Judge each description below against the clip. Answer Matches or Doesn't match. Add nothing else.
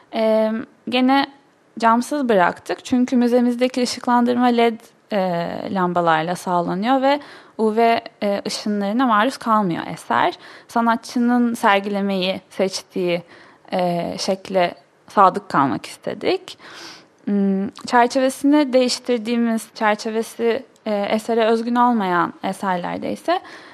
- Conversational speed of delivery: Doesn't match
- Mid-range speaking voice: Doesn't match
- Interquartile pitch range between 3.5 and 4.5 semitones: Matches